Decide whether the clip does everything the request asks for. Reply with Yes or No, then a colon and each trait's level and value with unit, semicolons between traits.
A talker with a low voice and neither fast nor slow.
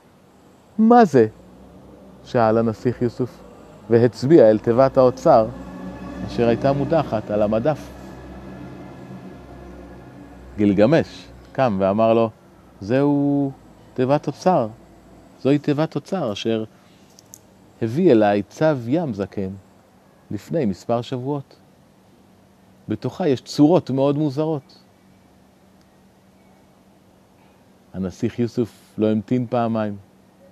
No: low, 115 Hz; slow, 85 wpm